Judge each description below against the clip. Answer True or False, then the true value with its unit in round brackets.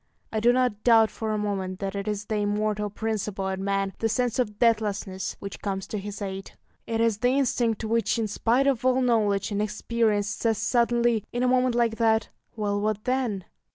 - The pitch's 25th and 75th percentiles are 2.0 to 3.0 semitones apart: True (2.5 semitones)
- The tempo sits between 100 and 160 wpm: False (200 wpm)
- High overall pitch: True (215 Hz)